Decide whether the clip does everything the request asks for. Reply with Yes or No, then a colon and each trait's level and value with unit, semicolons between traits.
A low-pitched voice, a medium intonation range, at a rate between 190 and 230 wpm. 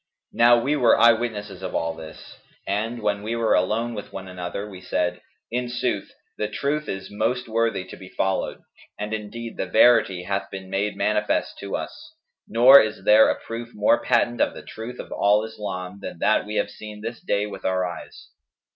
Yes: low, 105 Hz; average, 3.3 semitones; average, 195 wpm